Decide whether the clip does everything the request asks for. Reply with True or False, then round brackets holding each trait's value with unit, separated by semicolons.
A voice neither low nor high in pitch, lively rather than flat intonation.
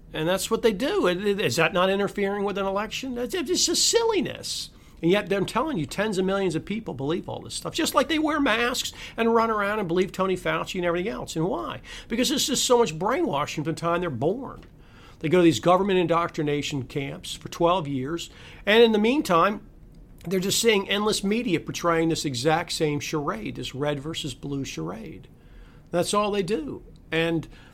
False (180 Hz; 4.8 semitones)